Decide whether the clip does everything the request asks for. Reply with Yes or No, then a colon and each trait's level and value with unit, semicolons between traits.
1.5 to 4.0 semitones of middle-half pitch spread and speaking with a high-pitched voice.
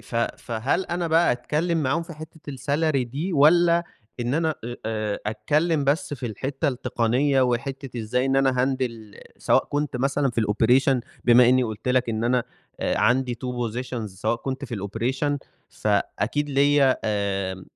No: average, 3.7 semitones; low, 130 Hz